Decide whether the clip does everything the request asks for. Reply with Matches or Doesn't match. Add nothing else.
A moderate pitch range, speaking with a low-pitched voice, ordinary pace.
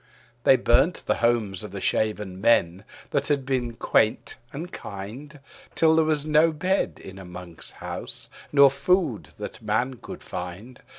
Doesn't match